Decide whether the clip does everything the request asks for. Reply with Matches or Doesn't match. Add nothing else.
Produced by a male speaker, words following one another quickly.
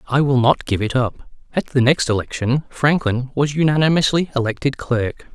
Doesn't match